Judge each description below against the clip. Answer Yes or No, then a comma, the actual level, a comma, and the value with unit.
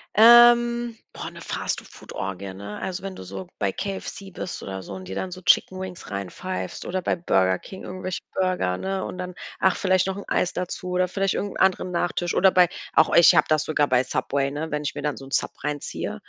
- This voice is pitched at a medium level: Yes, medium, 180 Hz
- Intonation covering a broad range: Yes, wide, 5.8 semitones